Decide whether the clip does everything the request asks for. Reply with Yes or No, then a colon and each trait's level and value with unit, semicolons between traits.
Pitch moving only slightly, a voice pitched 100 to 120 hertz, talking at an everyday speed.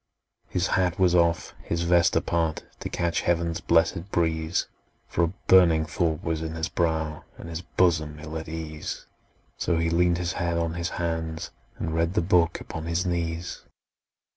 No: narrow, 1.2 semitones; very low, 85 Hz; average, 170 wpm